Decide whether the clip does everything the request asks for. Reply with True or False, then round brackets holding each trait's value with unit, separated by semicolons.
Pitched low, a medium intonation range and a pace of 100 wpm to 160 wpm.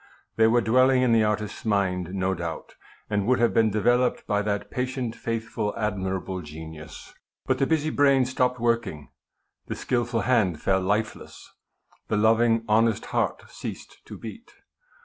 True (110 Hz; 3.5 semitones; 155 wpm)